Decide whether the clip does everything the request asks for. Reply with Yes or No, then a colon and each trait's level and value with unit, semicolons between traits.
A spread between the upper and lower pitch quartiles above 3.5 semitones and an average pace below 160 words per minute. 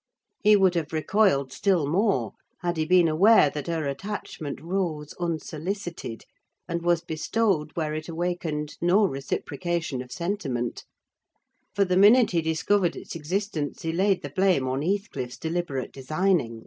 Yes: average, 4.2 semitones; average, 145 wpm